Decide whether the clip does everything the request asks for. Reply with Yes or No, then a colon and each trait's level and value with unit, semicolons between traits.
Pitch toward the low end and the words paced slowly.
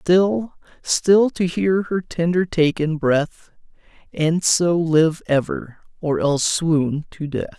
No: medium, 165 Hz; slow, 125 wpm